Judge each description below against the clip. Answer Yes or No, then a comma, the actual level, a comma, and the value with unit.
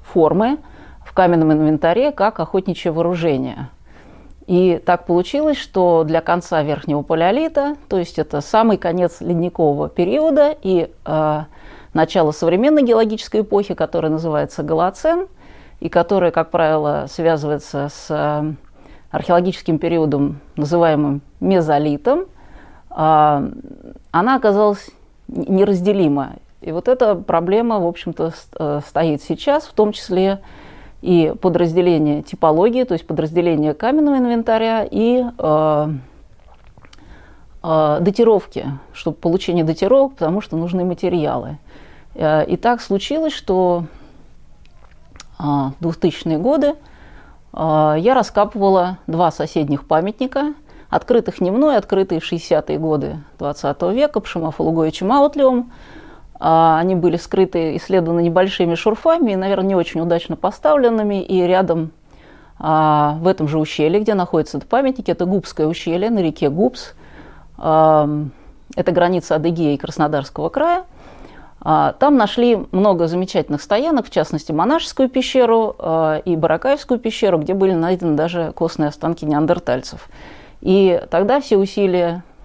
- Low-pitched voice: No, medium, 175 Hz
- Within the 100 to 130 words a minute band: Yes, average, 115 wpm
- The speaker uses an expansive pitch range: No, average, 4.9 semitones